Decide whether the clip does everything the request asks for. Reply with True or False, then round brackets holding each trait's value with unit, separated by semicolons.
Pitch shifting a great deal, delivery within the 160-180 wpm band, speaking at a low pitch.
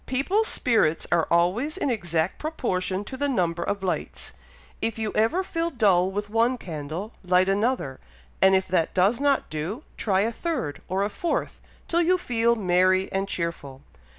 False (5.7 semitones; 170 wpm; 200 Hz)